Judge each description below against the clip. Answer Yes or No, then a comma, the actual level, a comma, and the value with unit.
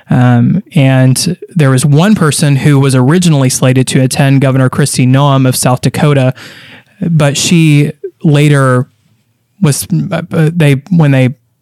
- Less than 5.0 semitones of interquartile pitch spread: Yes, average, 3.4 semitones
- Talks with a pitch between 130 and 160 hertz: Yes, medium, 140 Hz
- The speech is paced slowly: Yes, slow, 125 wpm